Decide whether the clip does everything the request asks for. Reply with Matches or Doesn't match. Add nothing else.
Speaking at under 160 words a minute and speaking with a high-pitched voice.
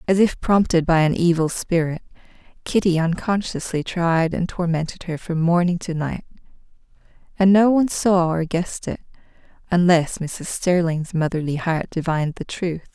Doesn't match